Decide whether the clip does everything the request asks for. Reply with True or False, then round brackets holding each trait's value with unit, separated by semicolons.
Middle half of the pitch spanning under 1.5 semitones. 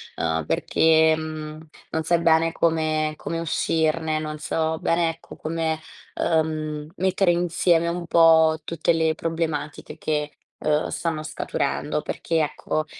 True (1.1 semitones)